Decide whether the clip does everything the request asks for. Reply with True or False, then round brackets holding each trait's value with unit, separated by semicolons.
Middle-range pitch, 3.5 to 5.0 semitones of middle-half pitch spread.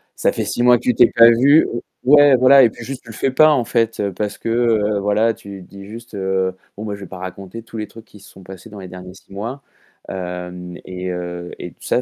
False (105 Hz; 4.1 semitones)